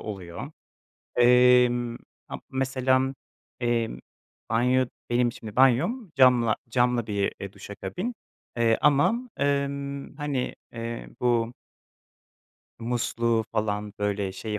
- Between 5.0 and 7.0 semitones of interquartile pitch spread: No, average, 2.8 semitones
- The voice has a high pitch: No, low, 120 Hz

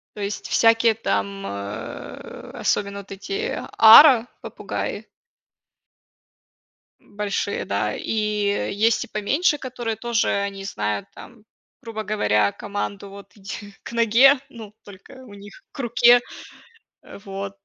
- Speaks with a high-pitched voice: Yes, high, 210 Hz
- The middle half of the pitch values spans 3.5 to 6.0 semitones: No, average, 2.8 semitones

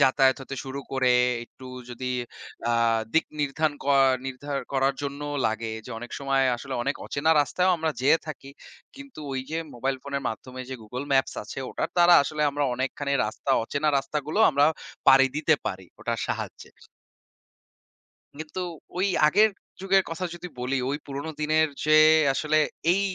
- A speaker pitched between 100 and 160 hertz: Yes, medium, 140 Hz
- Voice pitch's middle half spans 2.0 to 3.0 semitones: Yes, average, 2.7 semitones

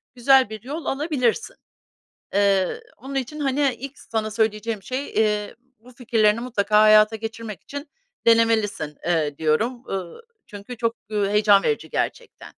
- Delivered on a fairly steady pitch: No, average, 3.7 semitones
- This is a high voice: Yes, high, 225 Hz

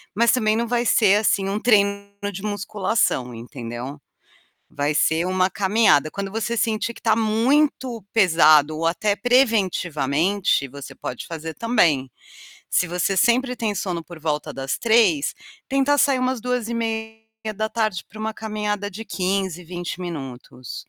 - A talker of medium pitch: No, high, 200 Hz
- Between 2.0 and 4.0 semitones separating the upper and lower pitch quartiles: No, average, 5.3 semitones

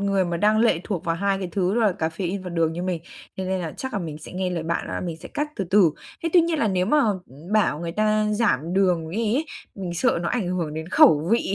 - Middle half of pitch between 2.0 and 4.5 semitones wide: Yes, average, 4.1 semitones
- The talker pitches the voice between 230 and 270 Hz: No, medium, 185 Hz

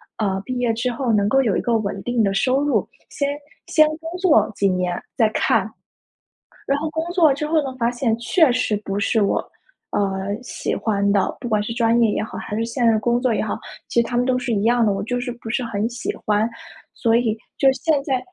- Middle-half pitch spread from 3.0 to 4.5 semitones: Yes, average, 3.4 semitones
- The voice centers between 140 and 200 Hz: No, high, 235 Hz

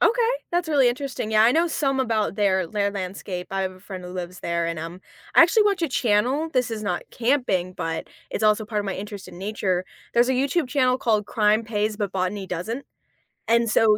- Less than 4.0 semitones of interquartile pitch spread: No, average, 5.1 semitones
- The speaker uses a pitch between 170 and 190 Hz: No, high, 215 Hz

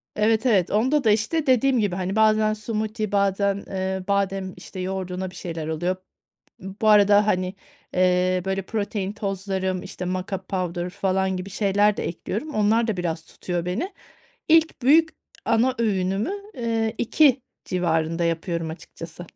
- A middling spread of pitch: Yes, average, 3.0 semitones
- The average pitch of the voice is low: No, high, 195 Hz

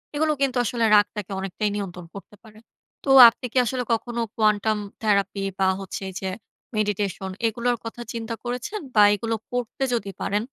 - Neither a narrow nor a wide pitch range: Yes, average, 3.1 semitones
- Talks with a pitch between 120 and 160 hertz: No, high, 215 Hz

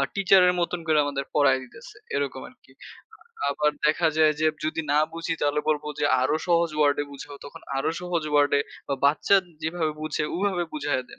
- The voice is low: No, medium, 155 Hz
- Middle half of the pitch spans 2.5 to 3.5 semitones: Yes, average, 2.9 semitones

